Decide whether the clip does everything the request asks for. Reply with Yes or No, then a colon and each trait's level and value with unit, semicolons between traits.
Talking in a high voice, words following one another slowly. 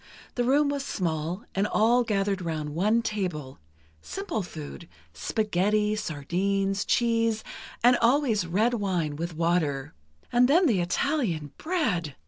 Yes: high, 200 Hz; slow, 125 wpm